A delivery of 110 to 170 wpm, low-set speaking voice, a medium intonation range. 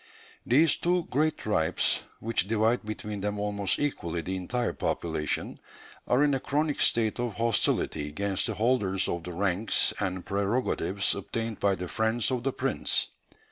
Yes: average, 155 wpm; low, 105 Hz; average, 4.3 semitones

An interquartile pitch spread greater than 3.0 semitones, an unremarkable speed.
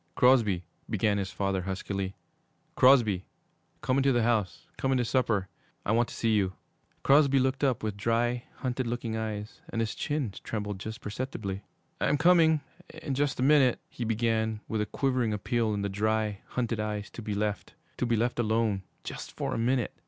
Yes: average, 3.4 semitones; average, 180 wpm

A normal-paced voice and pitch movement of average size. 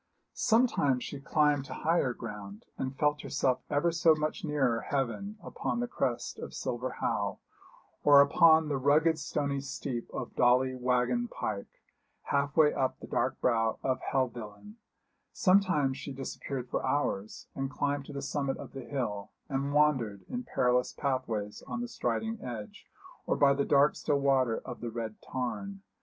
Yes: average, 160 wpm; average, 3.2 semitones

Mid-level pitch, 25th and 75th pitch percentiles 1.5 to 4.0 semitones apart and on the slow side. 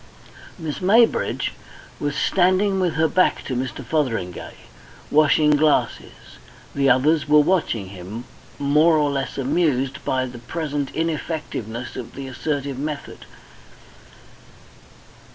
Yes: medium, 145 Hz; average, 3.7 semitones; slow, 115 wpm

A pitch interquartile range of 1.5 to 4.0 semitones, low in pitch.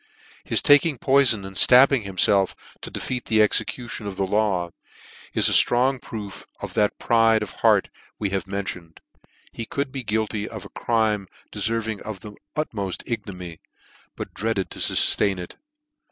Yes: average, 3.3 semitones; low, 110 Hz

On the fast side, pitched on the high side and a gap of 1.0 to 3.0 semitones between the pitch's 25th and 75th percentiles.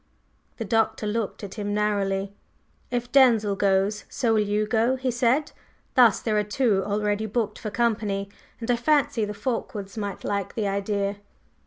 No: average, 165 wpm; high, 210 Hz; narrow, 2.6 semitones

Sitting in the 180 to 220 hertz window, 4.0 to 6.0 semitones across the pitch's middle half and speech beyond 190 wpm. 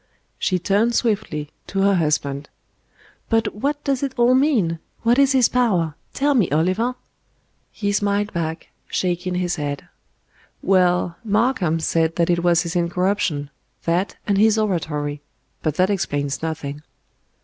No: medium, 185 Hz; average, 5.1 semitones; average, 140 wpm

